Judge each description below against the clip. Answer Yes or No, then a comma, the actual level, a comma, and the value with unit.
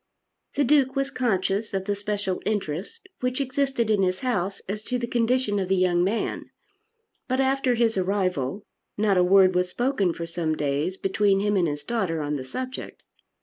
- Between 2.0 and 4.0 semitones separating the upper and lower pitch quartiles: No, average, 5.2 semitones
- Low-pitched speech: No, high, 200 Hz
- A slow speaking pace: No, average, 185 wpm